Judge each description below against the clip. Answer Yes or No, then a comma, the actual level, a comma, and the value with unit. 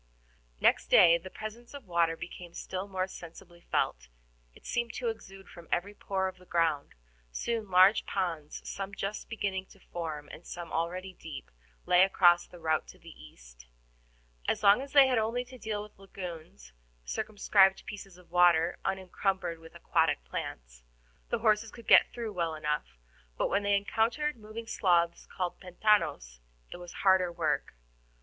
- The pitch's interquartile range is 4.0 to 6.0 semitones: No, average, 3.6 semitones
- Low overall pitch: No, medium, 185 Hz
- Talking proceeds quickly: No, average, 165 wpm